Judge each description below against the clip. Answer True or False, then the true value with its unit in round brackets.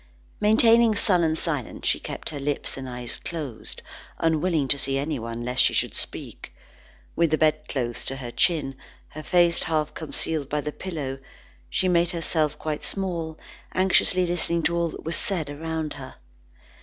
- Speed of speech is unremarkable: True (160 wpm)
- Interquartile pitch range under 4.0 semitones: True (3.4 semitones)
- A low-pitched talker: False (155 Hz)